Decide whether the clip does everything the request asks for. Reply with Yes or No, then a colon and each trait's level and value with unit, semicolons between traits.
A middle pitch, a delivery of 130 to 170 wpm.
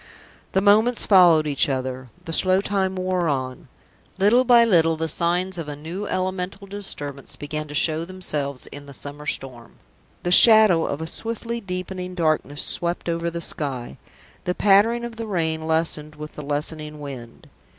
Yes: medium, 165 Hz; average, 165 wpm